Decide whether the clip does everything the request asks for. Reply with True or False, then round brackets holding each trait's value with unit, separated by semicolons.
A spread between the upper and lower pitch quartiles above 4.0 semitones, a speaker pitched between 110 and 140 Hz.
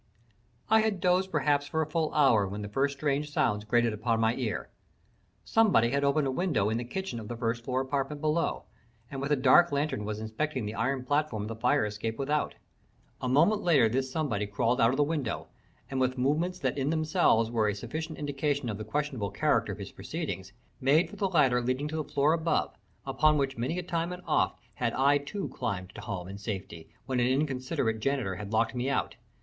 True (5.1 semitones; 135 Hz)